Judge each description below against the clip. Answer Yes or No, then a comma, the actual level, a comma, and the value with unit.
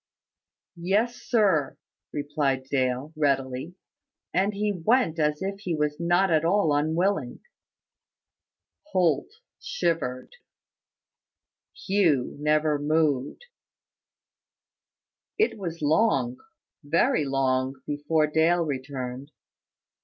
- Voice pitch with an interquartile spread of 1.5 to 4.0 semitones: No, average, 4.4 semitones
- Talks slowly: Yes, slow, 85 wpm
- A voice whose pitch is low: No, medium, 155 Hz